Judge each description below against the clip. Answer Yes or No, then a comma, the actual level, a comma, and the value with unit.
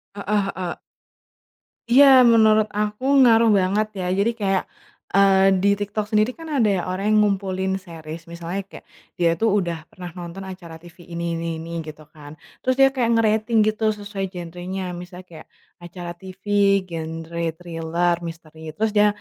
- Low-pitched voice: No, medium, 185 Hz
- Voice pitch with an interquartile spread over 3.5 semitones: Yes, average, 3.9 semitones